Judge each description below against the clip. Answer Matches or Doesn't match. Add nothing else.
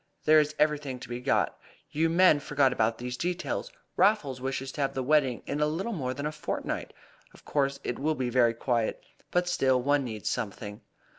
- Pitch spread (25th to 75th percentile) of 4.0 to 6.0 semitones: Doesn't match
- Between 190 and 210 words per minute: Matches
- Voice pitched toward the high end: Doesn't match